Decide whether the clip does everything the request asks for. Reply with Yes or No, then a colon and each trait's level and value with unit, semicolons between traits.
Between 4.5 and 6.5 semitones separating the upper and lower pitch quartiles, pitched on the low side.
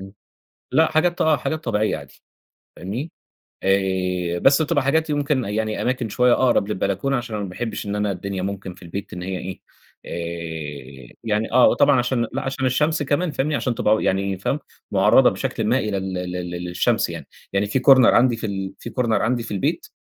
Yes: wide, 5.6 semitones; low, 105 Hz